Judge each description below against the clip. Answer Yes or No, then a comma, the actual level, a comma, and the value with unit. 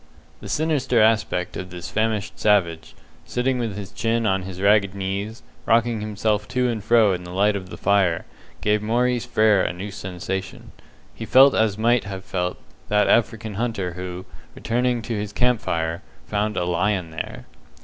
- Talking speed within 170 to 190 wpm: Yes, average, 175 wpm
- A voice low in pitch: Yes, low, 105 Hz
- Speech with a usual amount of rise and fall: Yes, average, 3.4 semitones